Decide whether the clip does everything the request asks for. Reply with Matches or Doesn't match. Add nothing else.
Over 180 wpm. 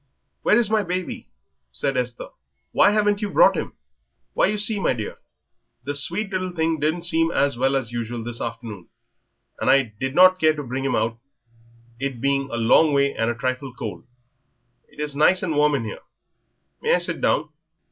Matches